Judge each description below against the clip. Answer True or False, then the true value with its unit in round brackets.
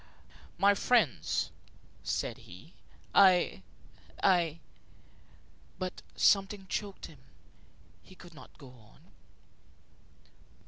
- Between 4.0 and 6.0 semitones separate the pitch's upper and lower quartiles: True (4.5 semitones)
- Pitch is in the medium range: True (180 Hz)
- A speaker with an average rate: False (90 wpm)